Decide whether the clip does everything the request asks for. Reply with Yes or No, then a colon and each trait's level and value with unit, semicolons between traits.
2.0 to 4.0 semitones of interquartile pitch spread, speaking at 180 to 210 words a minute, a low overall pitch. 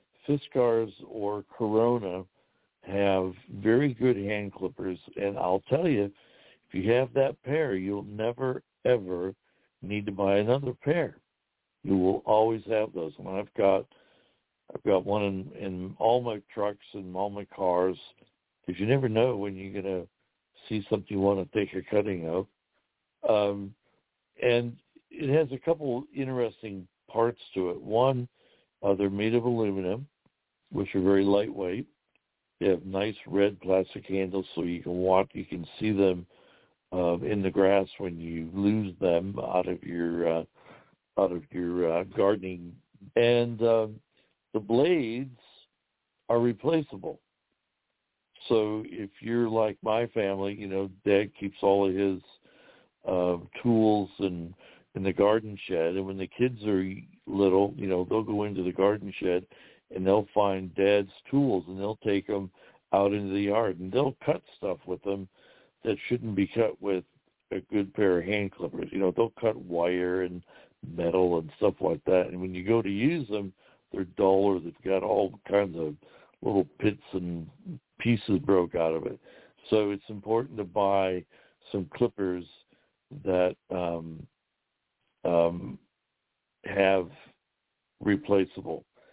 No: average, 2.9 semitones; average, 155 wpm; low, 100 Hz